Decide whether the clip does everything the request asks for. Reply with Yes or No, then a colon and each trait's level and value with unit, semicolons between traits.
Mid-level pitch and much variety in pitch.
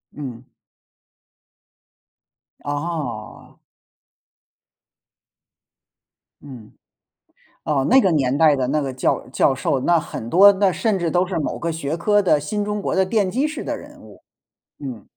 Yes: medium, 160 Hz; wide, 5.9 semitones